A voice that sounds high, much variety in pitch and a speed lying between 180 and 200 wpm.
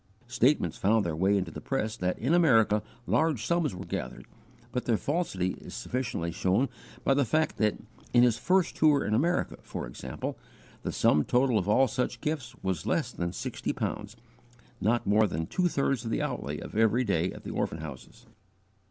No: low, 115 Hz; wide, 6.6 semitones; average, 185 wpm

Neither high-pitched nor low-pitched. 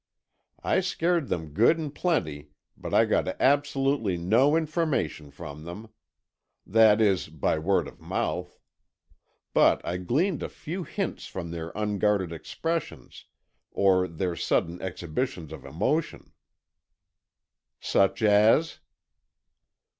No: low, 105 Hz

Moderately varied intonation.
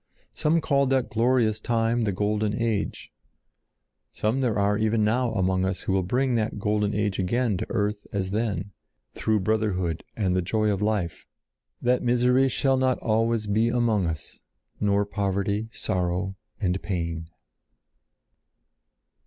Yes: average, 3.2 semitones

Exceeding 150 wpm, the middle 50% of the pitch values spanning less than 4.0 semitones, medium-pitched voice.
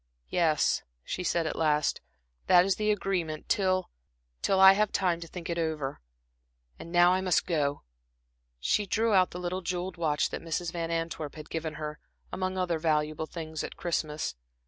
Yes: average, 175 wpm; average, 2.9 semitones; medium, 170 Hz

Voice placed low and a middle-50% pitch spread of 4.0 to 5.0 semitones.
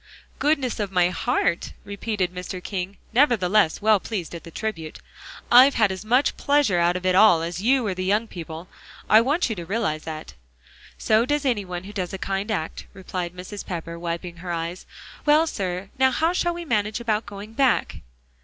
No: high, 200 Hz; average, 4.5 semitones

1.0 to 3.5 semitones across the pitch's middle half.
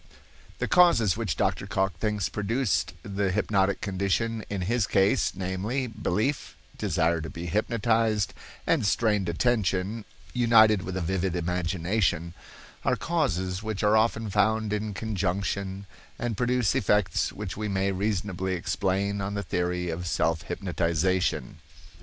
Yes: average, 3.1 semitones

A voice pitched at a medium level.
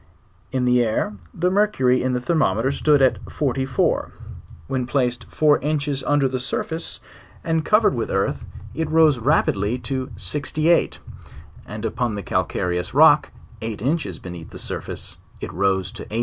No: low, 130 Hz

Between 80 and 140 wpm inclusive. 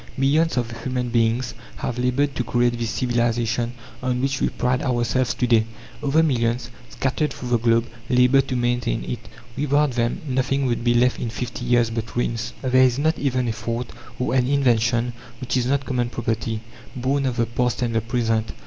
No: average, 190 wpm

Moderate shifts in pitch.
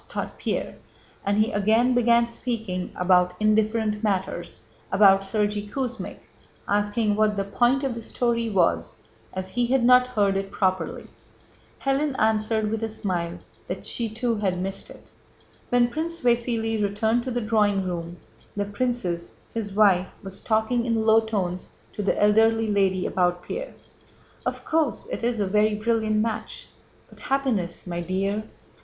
Yes: average, 3.2 semitones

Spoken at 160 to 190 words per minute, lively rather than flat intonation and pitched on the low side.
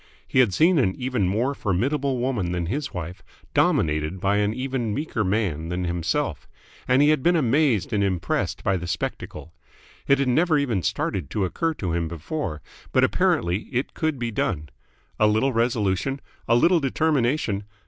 Yes: average, 170 wpm; wide, 7.0 semitones; low, 115 Hz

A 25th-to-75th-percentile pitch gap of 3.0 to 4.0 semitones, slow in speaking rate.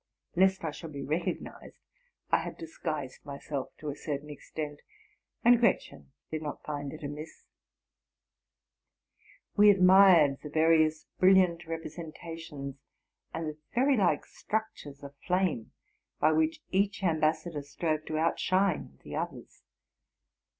Yes: average, 3.7 semitones; slow, 130 wpm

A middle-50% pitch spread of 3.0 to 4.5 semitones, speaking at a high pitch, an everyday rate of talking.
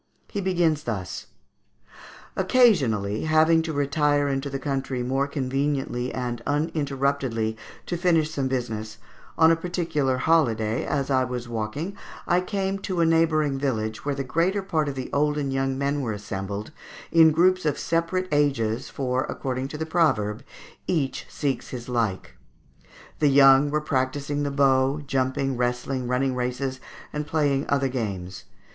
No: average, 3.7 semitones; medium, 140 Hz; average, 150 wpm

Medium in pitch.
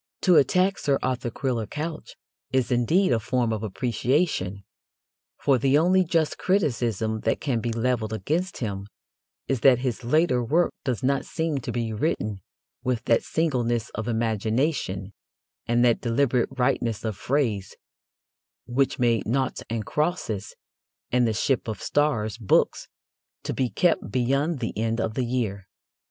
No: low, 125 Hz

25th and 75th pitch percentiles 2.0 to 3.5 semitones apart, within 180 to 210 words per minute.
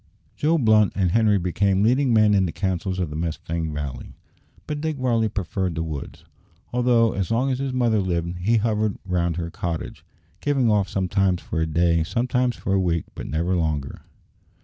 No: average, 5.3 semitones; average, 185 wpm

